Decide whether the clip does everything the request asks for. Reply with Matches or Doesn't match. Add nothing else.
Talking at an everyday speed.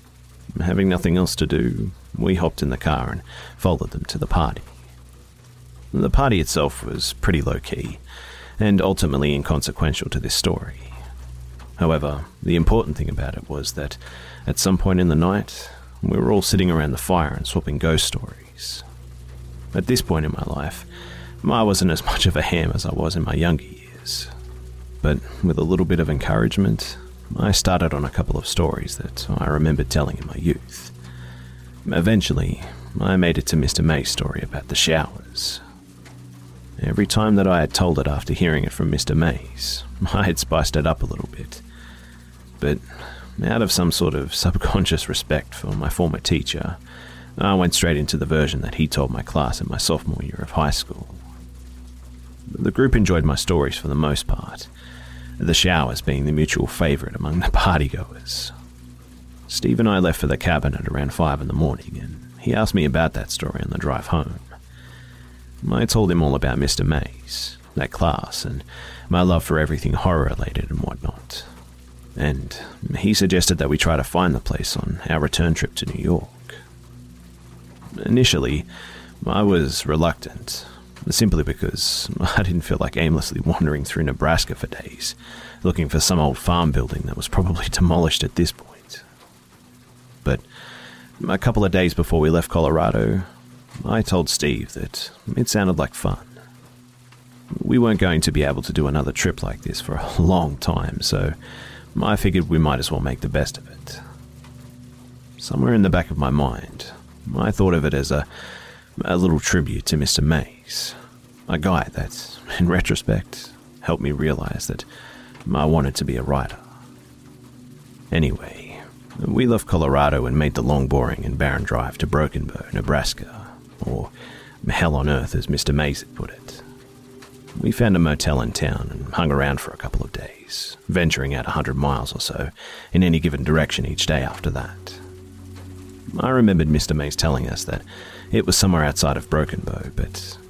Matches